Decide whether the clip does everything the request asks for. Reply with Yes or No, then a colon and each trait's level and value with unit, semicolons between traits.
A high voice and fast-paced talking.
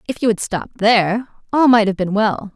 Yes: high, 215 Hz; fast, 235 wpm